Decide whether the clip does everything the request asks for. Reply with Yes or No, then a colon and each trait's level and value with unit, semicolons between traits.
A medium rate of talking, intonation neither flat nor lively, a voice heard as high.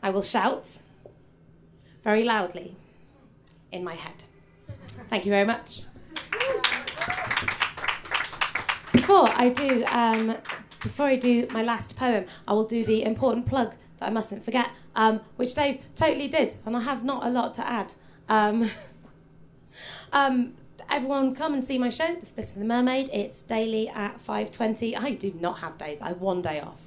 Yes: average, 165 wpm; average, 3.5 semitones; high, 230 Hz